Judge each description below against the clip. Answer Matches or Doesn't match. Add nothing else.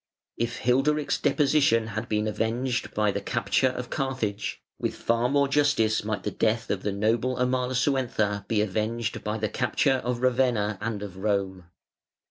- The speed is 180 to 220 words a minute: Doesn't match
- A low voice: Matches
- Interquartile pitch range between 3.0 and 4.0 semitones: Matches